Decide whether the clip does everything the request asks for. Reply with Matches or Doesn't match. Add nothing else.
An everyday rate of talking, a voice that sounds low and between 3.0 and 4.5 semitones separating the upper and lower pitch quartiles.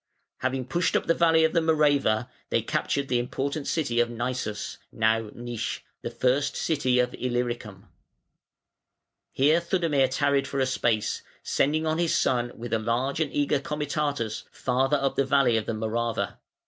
Matches